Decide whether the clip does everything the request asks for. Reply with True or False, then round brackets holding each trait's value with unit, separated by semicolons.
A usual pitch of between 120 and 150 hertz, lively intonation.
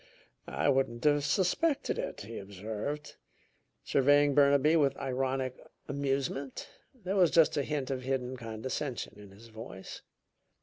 False (135 Hz; 3.2 semitones)